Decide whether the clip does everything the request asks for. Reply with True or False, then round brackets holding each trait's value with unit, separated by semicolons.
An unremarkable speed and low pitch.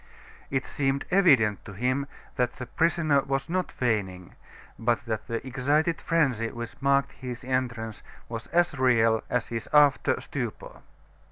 True (145 wpm; 130 Hz)